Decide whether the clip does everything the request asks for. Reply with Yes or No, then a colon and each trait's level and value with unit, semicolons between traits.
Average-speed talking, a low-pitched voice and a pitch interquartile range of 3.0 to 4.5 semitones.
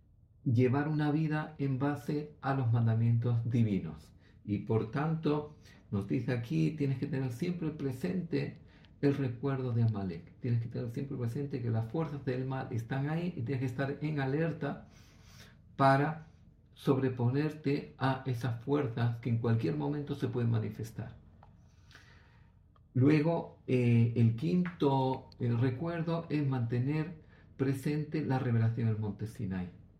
Yes: average, 135 wpm; low, 130 Hz; average, 4.1 semitones